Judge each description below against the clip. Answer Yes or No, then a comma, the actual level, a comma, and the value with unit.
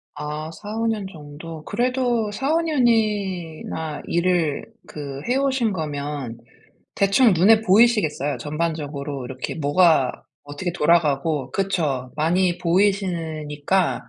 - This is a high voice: No, medium, 170 Hz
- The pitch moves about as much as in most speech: No, wide, 5.8 semitones